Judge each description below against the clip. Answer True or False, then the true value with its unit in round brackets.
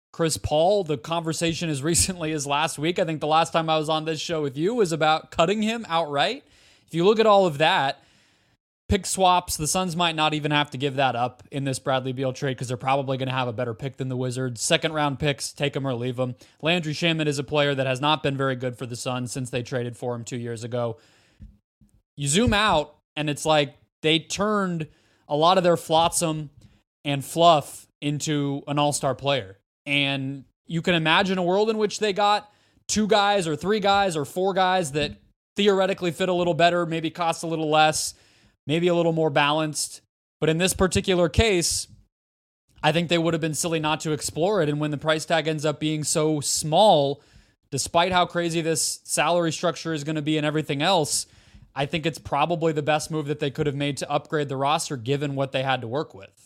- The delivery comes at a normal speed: False (220 wpm)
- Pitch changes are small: False (3.8 semitones)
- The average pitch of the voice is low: False (150 Hz)